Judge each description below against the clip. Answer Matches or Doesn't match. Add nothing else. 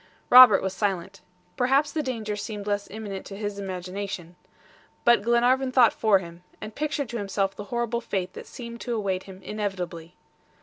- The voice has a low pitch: Doesn't match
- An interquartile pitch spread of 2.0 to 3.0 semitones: Doesn't match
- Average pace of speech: Matches